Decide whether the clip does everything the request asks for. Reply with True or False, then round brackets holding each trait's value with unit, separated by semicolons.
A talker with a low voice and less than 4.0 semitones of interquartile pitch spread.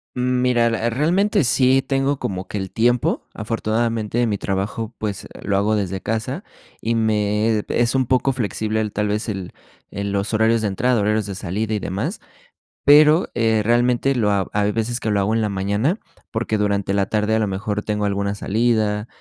True (110 Hz; 2.8 semitones)